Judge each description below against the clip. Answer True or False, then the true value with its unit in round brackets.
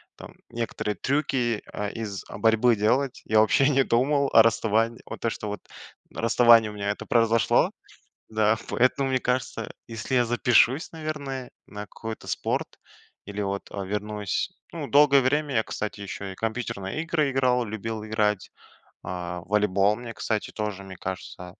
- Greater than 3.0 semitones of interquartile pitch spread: True (3.4 semitones)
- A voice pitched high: False (110 Hz)